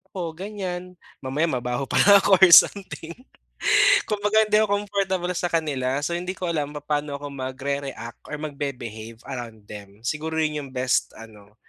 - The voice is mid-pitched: Yes, medium, 150 Hz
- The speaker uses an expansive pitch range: Yes, wide, 5.9 semitones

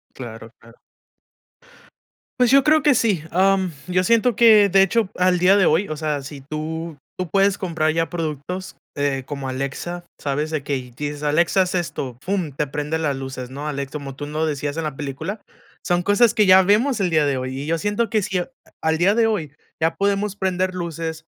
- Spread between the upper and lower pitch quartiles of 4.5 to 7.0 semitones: Yes, average, 5.0 semitones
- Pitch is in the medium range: Yes, medium, 165 Hz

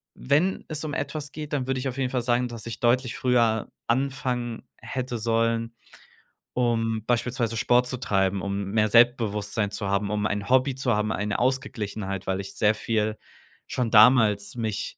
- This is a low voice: Yes, low, 115 Hz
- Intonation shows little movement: No, average, 3.1 semitones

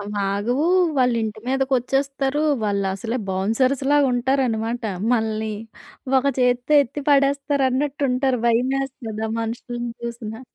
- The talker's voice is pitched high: Yes, high, 245 Hz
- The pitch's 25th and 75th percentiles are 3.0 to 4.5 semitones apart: Yes, average, 3.5 semitones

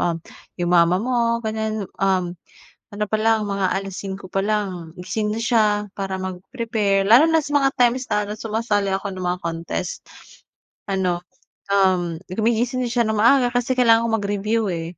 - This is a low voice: No, high, 210 Hz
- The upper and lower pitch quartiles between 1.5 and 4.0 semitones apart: Yes, average, 3.4 semitones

